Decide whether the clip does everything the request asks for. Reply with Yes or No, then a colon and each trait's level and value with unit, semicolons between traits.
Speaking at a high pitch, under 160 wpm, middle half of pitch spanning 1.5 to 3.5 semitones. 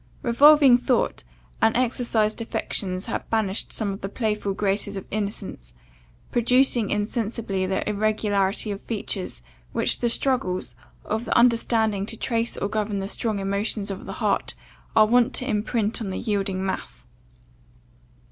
Yes: high, 215 Hz; average, 145 wpm; average, 2.8 semitones